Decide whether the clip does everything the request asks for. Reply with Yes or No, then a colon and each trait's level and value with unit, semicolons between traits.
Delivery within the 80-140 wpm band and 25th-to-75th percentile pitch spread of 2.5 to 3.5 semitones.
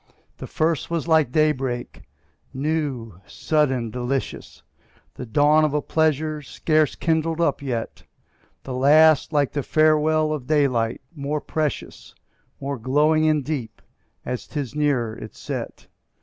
Yes: slow, 135 wpm; average, 3.2 semitones